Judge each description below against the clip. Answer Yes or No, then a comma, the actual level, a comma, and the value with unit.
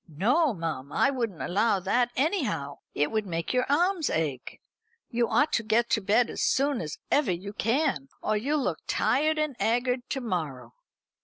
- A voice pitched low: No, high, 230 Hz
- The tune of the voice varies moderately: No, wide, 7.7 semitones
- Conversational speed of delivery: Yes, average, 175 wpm